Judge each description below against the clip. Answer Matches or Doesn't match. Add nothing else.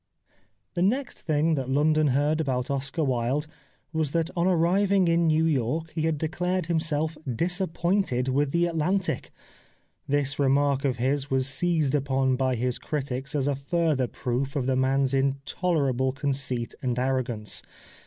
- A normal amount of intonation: Matches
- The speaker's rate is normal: Matches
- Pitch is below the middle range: Doesn't match